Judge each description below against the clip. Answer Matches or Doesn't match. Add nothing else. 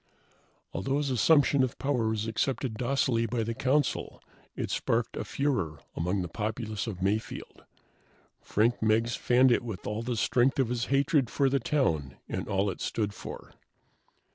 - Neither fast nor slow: Matches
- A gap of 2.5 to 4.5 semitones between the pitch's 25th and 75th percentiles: Matches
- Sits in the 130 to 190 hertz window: Doesn't match